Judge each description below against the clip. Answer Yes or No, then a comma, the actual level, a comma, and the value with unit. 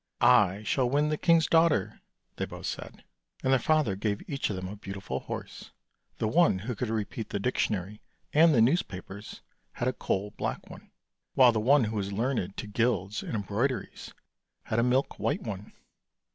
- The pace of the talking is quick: No, average, 185 wpm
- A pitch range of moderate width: Yes, average, 5.0 semitones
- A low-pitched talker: Yes, low, 110 Hz